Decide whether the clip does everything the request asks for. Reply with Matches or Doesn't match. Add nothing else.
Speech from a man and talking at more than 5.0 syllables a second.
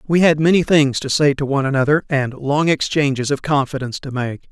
Matches